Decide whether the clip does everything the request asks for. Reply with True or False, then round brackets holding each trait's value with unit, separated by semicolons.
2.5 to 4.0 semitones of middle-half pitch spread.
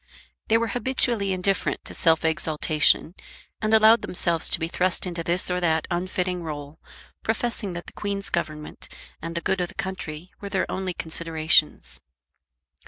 True (3.4 semitones)